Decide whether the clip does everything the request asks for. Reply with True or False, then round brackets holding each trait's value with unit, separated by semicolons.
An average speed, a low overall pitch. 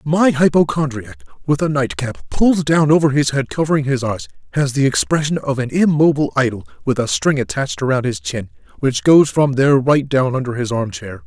True (190 wpm; 130 Hz)